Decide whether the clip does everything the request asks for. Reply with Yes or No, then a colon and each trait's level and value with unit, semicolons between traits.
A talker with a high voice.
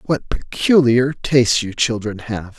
No: low, 120 Hz